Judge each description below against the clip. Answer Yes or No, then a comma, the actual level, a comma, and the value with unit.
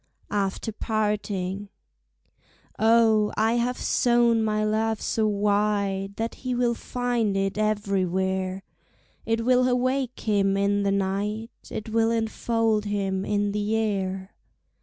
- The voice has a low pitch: No, high, 210 Hz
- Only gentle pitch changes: Yes, narrow, 2.3 semitones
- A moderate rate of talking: No, slow, 120 wpm